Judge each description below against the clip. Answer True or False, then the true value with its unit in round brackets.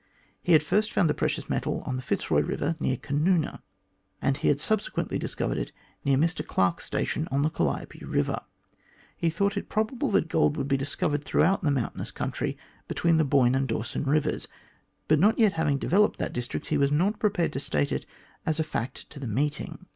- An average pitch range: True (4.3 semitones)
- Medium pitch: True (150 Hz)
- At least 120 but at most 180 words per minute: False (205 wpm)